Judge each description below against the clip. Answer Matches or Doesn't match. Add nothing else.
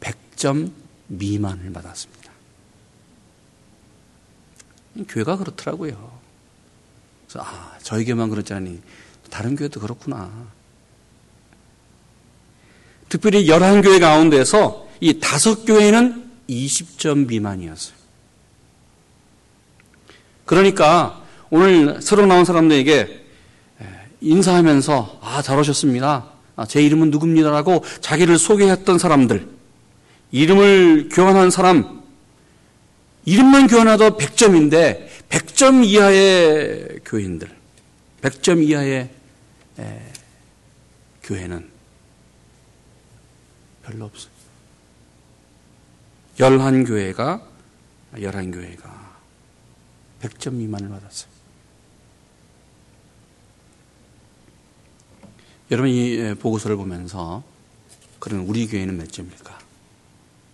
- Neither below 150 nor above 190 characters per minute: Matches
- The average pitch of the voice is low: Matches